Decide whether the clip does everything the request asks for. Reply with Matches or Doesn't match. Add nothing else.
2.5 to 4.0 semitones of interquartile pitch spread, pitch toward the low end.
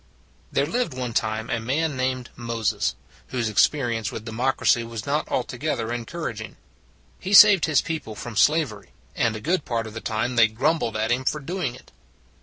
Doesn't match